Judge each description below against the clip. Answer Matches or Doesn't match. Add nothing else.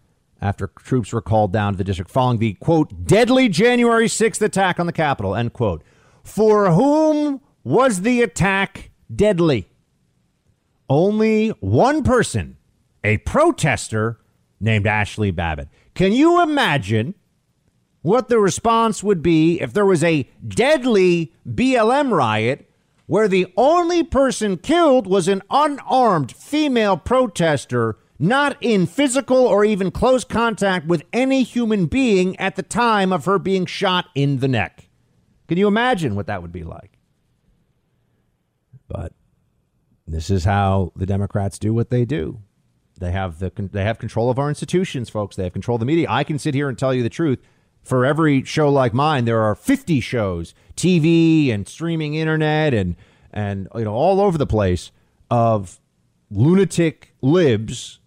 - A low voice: Doesn't match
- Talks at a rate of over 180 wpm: Doesn't match